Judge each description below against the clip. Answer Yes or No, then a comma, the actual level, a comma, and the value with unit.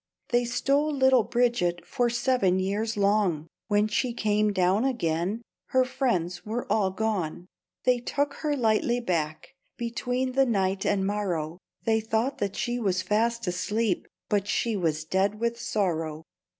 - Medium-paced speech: Yes, average, 150 wpm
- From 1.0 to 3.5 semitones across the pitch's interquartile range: No, average, 4.5 semitones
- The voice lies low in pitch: No, high, 215 Hz